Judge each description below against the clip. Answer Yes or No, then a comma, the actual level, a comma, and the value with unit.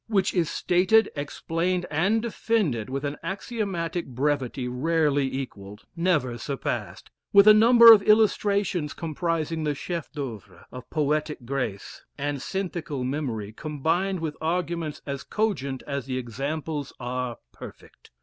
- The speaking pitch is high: No, medium, 155 Hz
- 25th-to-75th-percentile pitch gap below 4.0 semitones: No, average, 5.1 semitones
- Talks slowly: Yes, slow, 130 wpm